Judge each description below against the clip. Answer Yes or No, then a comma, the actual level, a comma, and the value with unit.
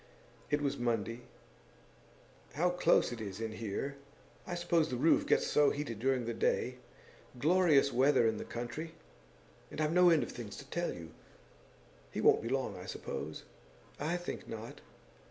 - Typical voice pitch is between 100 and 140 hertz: Yes, low, 135 Hz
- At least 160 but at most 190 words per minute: Yes, average, 165 wpm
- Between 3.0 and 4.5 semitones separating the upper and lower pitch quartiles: No, wide, 5.6 semitones